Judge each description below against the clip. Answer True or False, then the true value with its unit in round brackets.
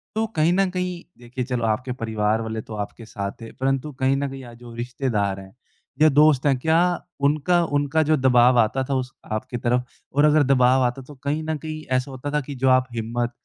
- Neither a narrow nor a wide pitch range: True (3.9 semitones)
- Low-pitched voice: True (130 Hz)